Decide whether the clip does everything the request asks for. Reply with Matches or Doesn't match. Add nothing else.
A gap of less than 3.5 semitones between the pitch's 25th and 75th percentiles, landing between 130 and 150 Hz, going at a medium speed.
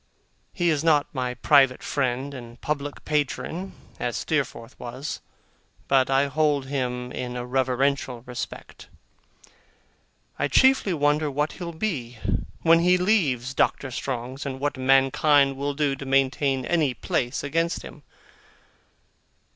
Doesn't match